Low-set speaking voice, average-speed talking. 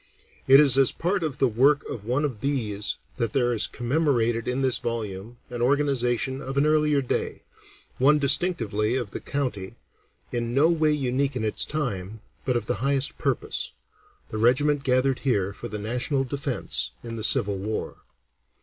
Yes: low, 125 Hz; average, 170 wpm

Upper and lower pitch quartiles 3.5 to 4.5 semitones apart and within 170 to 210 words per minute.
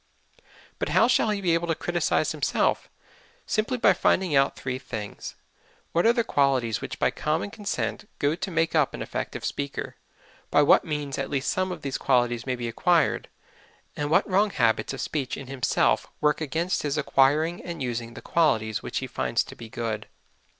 No: average, 5.1 semitones; average, 185 wpm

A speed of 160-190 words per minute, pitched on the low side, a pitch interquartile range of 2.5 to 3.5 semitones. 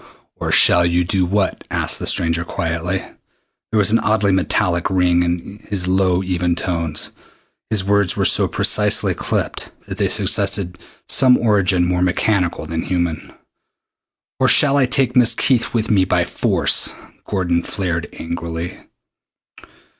No: average, 145 wpm; very low, 90 Hz; average, 2.9 semitones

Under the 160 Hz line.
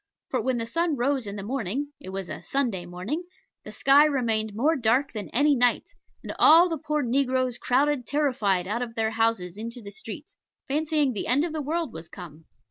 No: high, 245 Hz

